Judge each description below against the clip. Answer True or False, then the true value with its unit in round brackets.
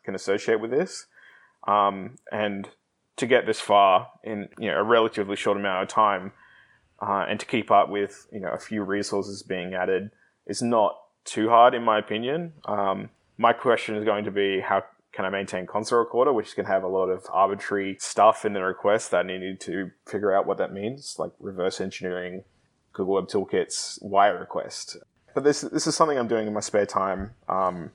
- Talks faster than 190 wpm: True (200 wpm)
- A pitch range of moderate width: False (2.1 semitones)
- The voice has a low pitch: True (100 Hz)